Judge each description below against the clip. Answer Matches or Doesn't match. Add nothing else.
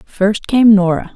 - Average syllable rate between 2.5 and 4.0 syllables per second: Matches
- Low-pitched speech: Doesn't match